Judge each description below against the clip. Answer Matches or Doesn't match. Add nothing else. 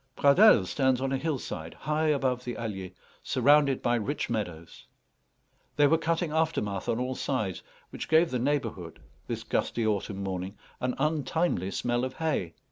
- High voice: Doesn't match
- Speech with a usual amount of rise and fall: Doesn't match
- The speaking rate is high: Doesn't match